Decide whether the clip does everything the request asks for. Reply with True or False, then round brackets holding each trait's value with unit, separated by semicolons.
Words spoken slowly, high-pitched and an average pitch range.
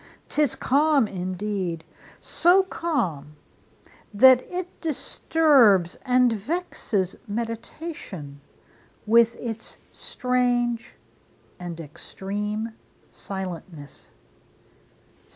False (65 wpm; 225 Hz; 6.0 semitones)